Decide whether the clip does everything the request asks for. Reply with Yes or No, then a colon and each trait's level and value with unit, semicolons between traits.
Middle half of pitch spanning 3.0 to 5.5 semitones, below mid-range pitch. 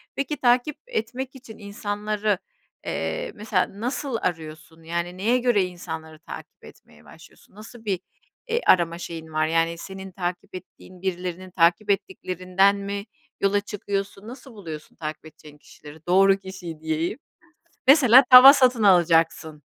No: average, 4.4 semitones; high, 190 Hz